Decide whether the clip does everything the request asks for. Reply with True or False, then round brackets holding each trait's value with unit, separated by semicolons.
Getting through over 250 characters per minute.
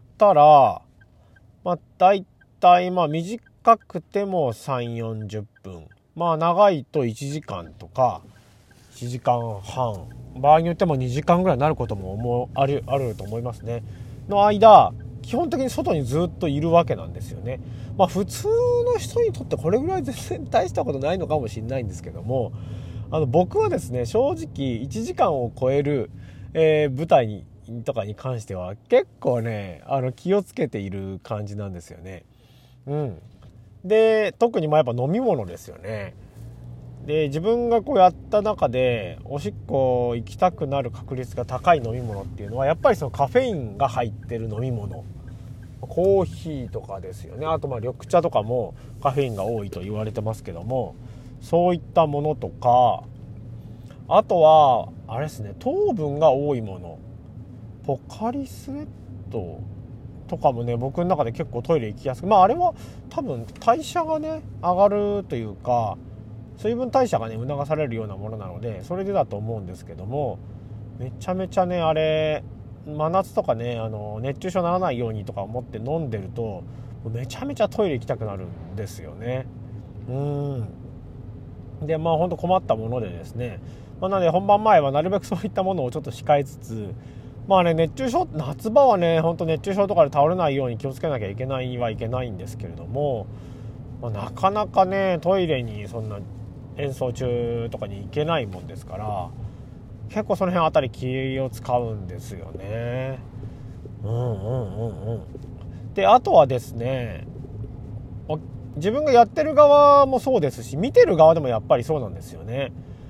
True (315 characters per minute)